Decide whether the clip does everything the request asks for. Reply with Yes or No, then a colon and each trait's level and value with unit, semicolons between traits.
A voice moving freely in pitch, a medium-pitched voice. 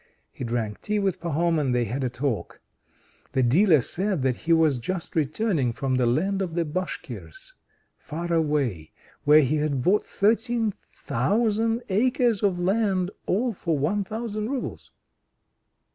Yes: wide, 7.1 semitones; medium, 170 Hz